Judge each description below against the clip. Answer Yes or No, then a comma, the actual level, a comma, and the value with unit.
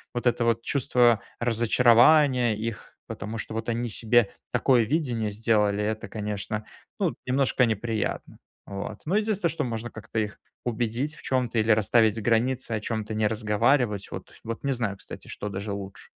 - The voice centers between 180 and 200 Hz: No, low, 115 Hz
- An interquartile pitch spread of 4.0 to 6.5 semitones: No, narrow, 2.4 semitones